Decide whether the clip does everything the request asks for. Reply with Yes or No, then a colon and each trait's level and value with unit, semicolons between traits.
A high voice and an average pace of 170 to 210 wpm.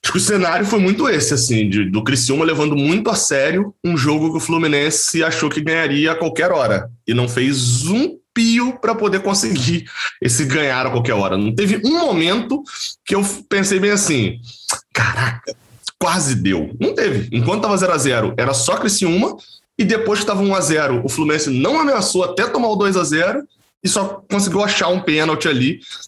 No: medium, 165 Hz; fast, 185 wpm